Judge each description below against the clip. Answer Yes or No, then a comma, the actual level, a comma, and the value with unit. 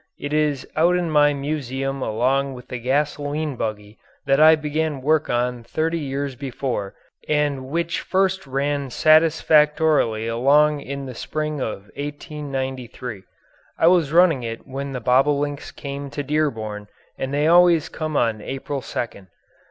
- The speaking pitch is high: No, medium, 140 Hz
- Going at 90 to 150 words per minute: Yes, average, 145 wpm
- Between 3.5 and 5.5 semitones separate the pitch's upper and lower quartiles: No, average, 3.0 semitones